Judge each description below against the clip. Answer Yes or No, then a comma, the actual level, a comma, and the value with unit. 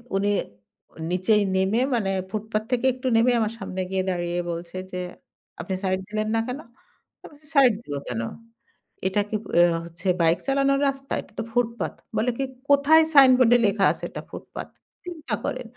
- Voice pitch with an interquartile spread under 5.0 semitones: No, wide, 5.6 semitones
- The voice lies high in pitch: Yes, high, 220 Hz